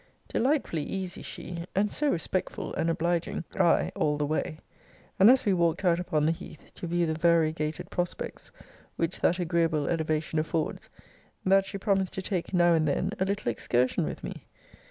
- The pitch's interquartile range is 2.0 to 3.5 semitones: Yes, average, 2.9 semitones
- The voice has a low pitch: No, medium, 170 Hz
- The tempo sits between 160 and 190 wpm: Yes, average, 175 wpm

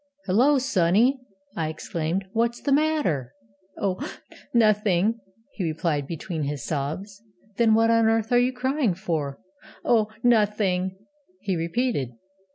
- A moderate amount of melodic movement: No, wide, 6.0 semitones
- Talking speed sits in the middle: No, slow, 120 wpm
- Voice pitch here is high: Yes, high, 205 Hz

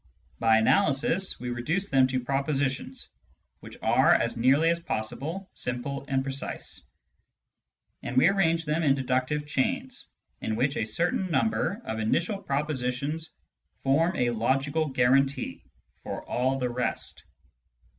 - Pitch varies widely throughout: No, average, 4.2 semitones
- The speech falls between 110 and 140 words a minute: Yes, slow, 135 wpm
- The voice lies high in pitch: No, low, 135 Hz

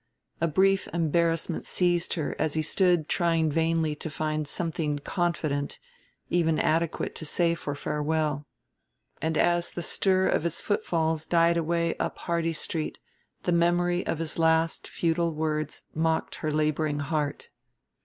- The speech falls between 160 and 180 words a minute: No, average, 145 wpm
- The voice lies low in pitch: No, medium, 165 Hz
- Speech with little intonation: Yes, narrow, 1.8 semitones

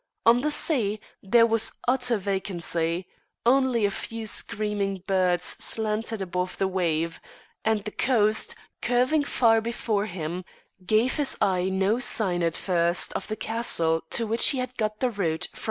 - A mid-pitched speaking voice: No, high, 210 Hz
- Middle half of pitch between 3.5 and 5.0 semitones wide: Yes, average, 4.1 semitones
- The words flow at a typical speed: Yes, average, 160 wpm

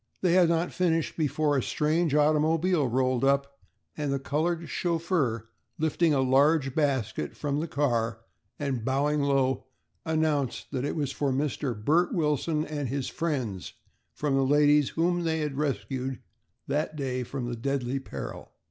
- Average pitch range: Yes, average, 3.0 semitones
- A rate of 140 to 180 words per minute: Yes, average, 150 wpm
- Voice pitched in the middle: Yes, medium, 145 Hz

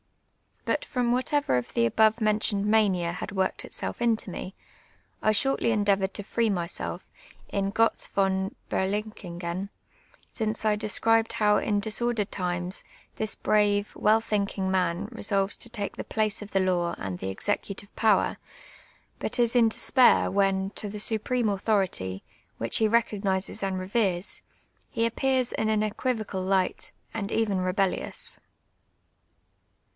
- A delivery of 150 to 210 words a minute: No, average, 140 wpm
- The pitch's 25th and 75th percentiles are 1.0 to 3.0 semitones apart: Yes, narrow, 2.6 semitones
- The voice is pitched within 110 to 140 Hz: No, high, 205 Hz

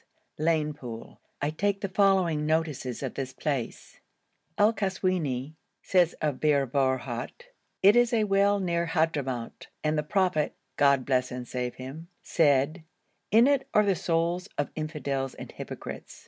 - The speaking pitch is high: No, medium, 155 Hz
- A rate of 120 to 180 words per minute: Yes, average, 145 wpm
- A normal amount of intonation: No, wide, 5.7 semitones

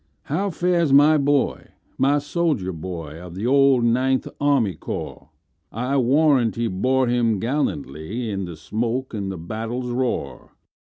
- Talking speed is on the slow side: Yes, slow, 120 wpm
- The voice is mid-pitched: No, low, 120 Hz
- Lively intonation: Yes, wide, 6.5 semitones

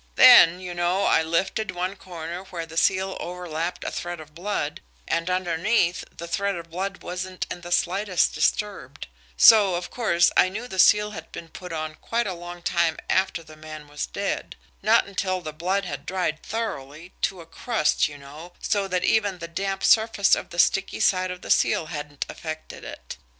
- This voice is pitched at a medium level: Yes, medium, 175 Hz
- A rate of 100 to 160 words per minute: No, average, 190 wpm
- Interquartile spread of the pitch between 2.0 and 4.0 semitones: Yes, average, 2.7 semitones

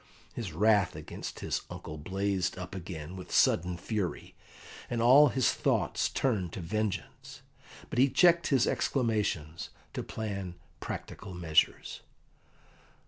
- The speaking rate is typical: No, slow, 125 wpm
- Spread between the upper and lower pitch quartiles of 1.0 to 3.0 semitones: No, average, 4.7 semitones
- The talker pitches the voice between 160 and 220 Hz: No, low, 100 Hz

